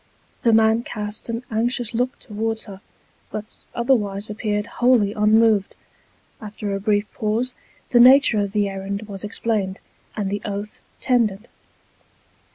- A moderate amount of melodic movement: No, narrow, 2.1 semitones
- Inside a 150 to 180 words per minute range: No, slow, 135 wpm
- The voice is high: Yes, high, 215 Hz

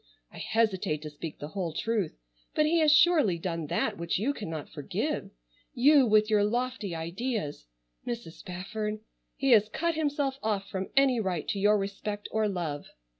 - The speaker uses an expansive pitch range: Yes, wide, 6.4 semitones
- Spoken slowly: No, average, 160 wpm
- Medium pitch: No, high, 210 Hz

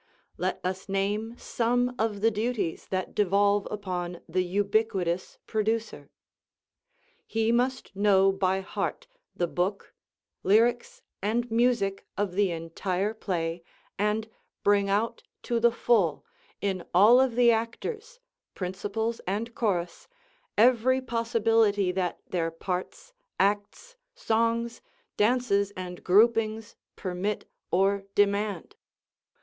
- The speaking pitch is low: No, high, 205 Hz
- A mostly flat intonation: No, average, 3.3 semitones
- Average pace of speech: No, slow, 110 wpm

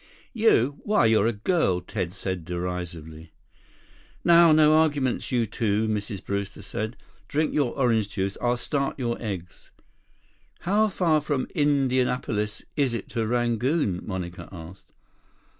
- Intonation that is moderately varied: No, wide, 6.7 semitones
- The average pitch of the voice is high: No, low, 115 Hz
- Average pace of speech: No, slow, 130 wpm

